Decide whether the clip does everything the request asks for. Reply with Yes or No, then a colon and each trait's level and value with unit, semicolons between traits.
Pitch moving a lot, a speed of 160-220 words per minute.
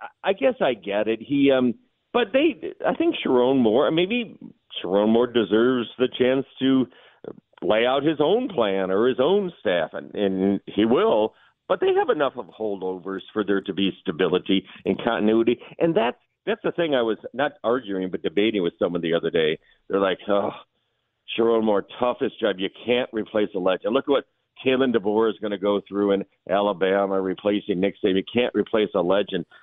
No: average, 4.8 semitones; average, 190 wpm